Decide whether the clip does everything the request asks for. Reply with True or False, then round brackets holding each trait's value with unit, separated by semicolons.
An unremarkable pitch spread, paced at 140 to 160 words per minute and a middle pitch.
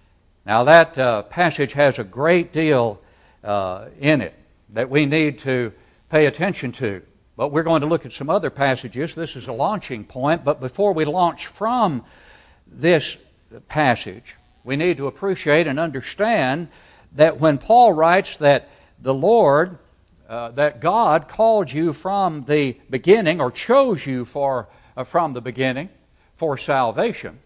True (4.5 semitones; 155 wpm; 145 Hz)